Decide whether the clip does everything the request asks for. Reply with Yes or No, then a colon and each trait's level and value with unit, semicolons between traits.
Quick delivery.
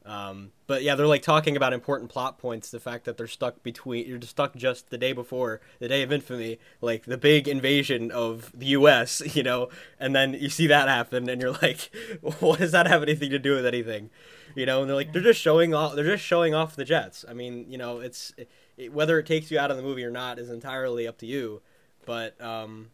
Yes: fast, 245 wpm